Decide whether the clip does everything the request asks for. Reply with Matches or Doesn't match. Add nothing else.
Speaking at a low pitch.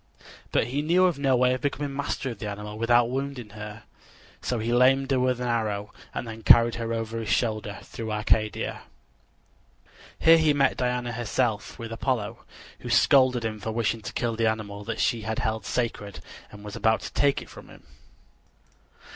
Matches